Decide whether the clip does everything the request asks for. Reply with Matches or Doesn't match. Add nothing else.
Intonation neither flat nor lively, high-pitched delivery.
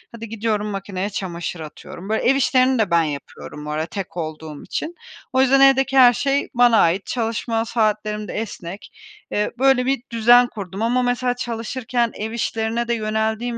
Matches